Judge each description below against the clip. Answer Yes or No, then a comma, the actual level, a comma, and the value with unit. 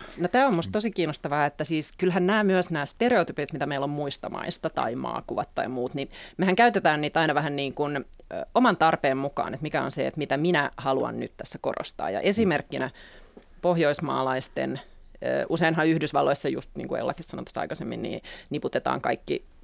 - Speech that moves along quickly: Yes, fast, 175 wpm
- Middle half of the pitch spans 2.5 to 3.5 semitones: No, average, 4.1 semitones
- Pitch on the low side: No, medium, 155 Hz